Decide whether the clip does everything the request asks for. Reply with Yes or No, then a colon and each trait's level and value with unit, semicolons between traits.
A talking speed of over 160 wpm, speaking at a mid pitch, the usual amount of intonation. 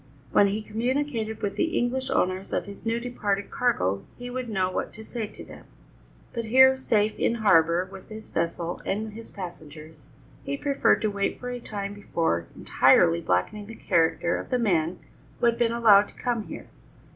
No: average, 185 wpm; high, 210 Hz; average, 4.6 semitones